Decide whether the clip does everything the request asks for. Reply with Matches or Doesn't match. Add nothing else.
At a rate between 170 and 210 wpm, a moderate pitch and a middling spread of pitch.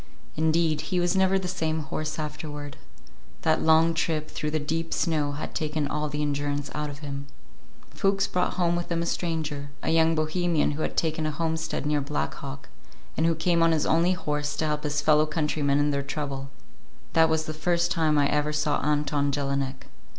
Doesn't match